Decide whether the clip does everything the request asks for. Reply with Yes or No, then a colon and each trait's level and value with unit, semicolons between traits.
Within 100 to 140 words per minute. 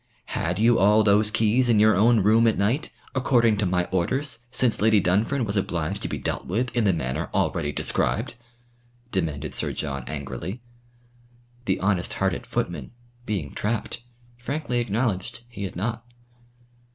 No: average, 155 wpm